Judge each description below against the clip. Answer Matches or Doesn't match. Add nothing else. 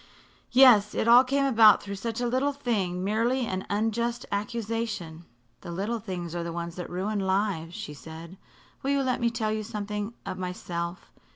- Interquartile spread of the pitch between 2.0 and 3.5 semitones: Doesn't match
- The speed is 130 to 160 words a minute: Doesn't match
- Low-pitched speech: Doesn't match